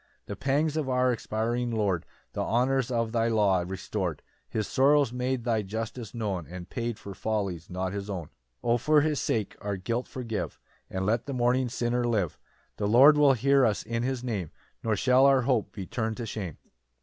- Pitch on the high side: No, low, 115 Hz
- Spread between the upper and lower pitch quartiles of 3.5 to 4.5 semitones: Yes, average, 3.9 semitones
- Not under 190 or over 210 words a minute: Yes, average, 195 wpm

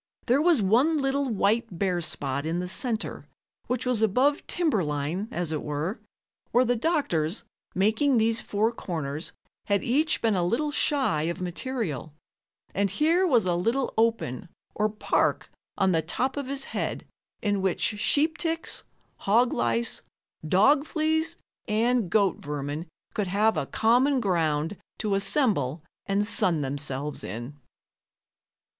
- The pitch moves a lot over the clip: Yes, wide, 7.3 semitones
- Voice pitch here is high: Yes, high, 210 Hz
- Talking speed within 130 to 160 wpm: Yes, average, 145 wpm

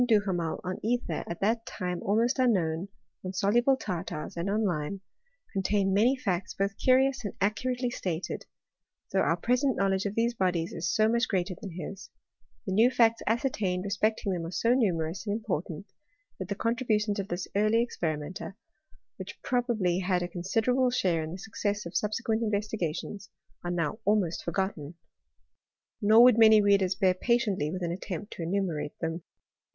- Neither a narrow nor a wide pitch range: Yes, average, 4.0 semitones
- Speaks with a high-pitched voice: Yes, high, 200 Hz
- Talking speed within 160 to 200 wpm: Yes, average, 175 wpm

